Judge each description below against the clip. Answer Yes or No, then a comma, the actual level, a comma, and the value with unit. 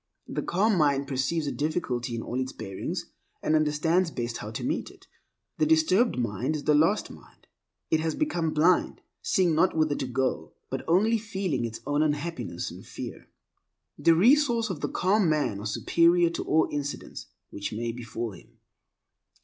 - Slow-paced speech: No, average, 175 wpm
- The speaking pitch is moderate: Yes, medium, 155 Hz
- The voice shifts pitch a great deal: Yes, wide, 5.9 semitones